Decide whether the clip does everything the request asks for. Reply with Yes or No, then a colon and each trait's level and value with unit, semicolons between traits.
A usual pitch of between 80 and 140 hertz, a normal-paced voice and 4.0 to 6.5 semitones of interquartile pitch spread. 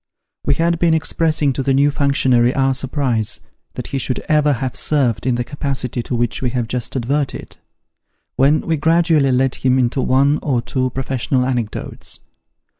No: low, 135 Hz; average, 170 wpm; narrow, 2.6 semitones